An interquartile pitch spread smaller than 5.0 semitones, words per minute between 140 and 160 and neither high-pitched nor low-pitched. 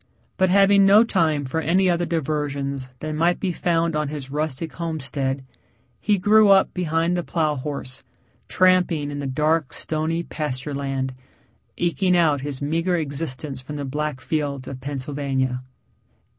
Yes: average, 3.6 semitones; average, 150 wpm; medium, 150 Hz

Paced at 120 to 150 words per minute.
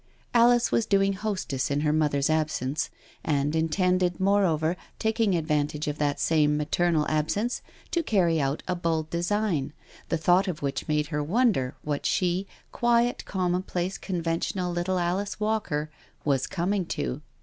Yes: average, 145 wpm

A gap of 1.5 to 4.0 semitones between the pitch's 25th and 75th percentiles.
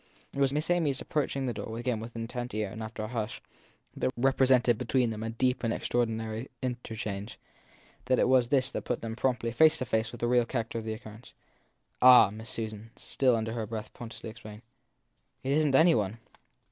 Yes: narrow, 2.6 semitones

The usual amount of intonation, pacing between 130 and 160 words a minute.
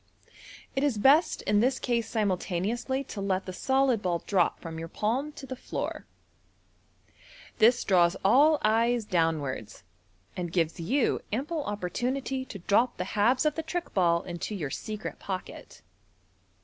No: wide, 6.4 semitones; average, 150 wpm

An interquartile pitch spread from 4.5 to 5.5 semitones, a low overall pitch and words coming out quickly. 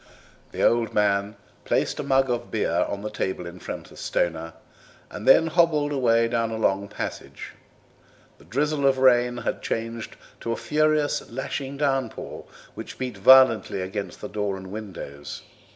No: average, 5.0 semitones; low, 115 Hz; average, 155 wpm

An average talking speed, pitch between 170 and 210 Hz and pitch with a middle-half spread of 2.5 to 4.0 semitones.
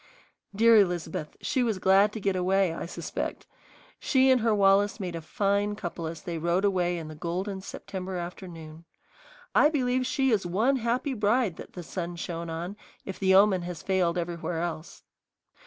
Yes: average, 175 wpm; high, 190 Hz; average, 3.4 semitones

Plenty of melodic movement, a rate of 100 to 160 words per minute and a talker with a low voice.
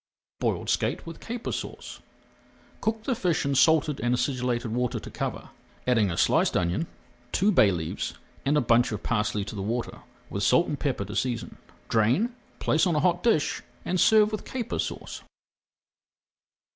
No: wide, 7.7 semitones; average, 170 wpm; low, 130 Hz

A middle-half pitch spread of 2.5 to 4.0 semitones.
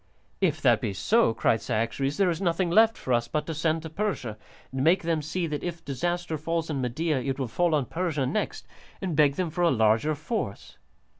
No: average, 4.6 semitones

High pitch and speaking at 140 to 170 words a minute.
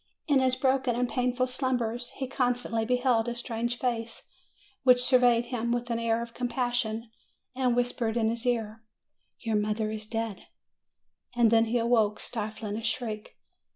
Yes: high, 235 Hz; average, 160 wpm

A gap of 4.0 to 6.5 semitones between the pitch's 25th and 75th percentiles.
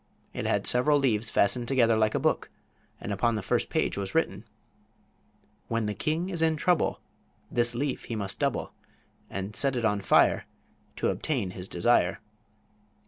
Yes: average, 5.1 semitones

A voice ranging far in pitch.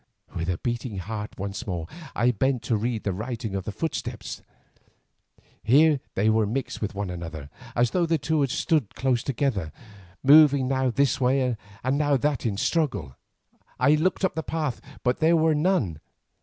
Yes: wide, 5.9 semitones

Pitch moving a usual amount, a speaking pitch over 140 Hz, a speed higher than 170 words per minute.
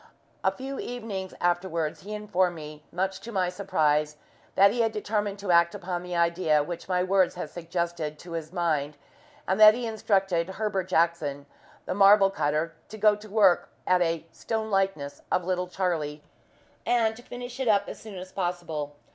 Yes: average, 3.5 semitones; medium, 185 Hz; average, 180 wpm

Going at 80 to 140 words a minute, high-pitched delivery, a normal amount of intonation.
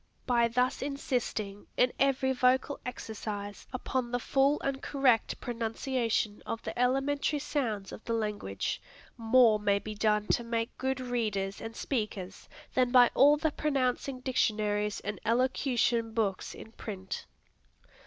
Yes: slow, 135 wpm; high, 235 Hz; average, 3.5 semitones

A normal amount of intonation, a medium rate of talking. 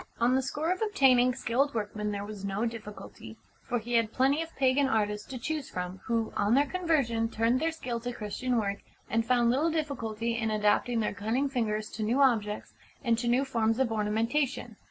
Yes: average, 3.7 semitones; average, 195 wpm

